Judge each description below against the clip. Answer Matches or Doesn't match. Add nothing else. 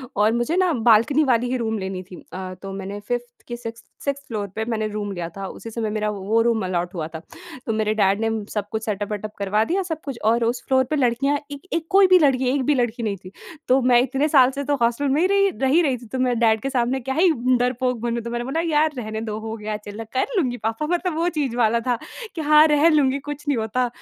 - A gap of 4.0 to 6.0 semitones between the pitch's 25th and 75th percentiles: Matches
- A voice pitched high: Matches